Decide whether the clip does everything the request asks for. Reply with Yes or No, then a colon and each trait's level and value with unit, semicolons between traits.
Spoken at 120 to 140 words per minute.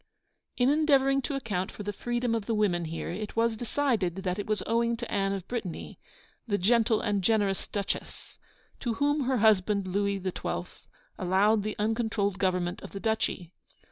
No: average, 175 wpm